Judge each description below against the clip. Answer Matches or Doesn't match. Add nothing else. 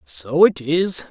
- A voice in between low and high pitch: Matches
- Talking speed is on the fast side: Doesn't match